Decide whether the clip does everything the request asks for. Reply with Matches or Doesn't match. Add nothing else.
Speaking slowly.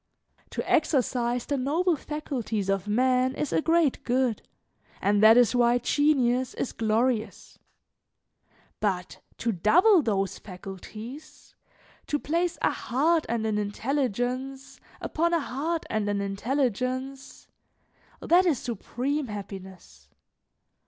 Matches